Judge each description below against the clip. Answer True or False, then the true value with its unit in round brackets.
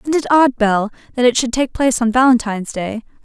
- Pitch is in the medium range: False (240 Hz)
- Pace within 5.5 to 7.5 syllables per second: True (6.0 syllables/s)